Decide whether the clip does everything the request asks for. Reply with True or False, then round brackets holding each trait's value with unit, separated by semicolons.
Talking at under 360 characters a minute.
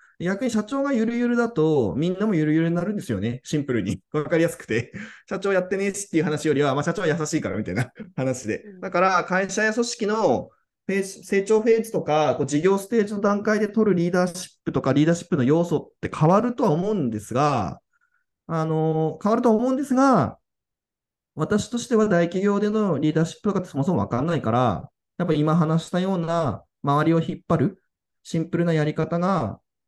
False (420 characters per minute)